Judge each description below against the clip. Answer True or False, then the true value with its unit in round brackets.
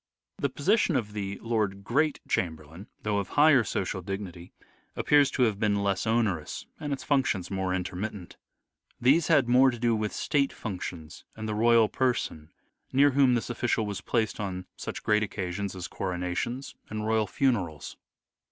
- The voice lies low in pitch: True (105 Hz)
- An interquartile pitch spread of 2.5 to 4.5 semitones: False (4.9 semitones)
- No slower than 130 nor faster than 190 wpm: True (160 wpm)